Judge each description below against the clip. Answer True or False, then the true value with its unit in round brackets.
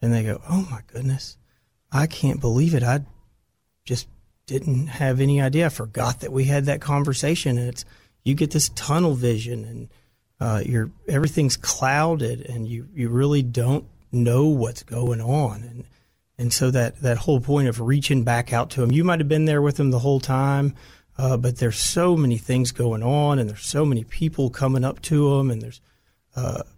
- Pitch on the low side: True (130 Hz)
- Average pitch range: True (3.2 semitones)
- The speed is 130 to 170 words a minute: False (195 wpm)